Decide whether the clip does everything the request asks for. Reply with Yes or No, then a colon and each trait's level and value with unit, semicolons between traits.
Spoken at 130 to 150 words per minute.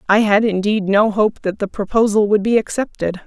No: average, 200 wpm